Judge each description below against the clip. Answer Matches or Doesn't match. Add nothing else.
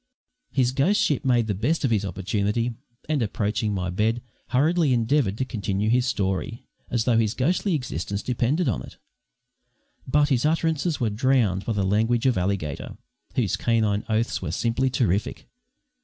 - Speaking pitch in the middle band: Doesn't match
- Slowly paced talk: Doesn't match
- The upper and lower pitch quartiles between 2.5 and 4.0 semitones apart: Doesn't match